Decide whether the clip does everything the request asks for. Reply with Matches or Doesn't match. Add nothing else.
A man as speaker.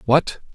Matches